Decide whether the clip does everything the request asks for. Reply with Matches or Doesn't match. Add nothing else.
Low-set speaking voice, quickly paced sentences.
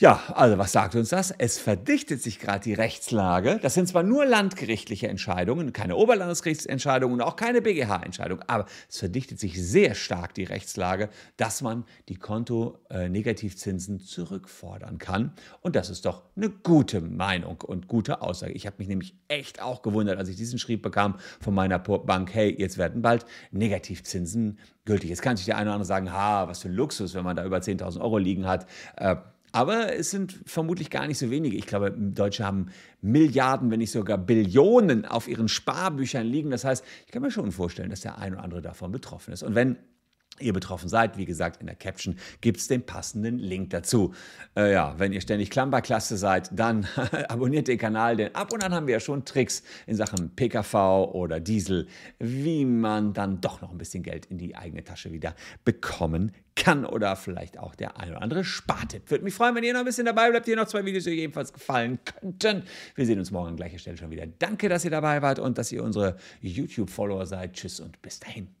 Matches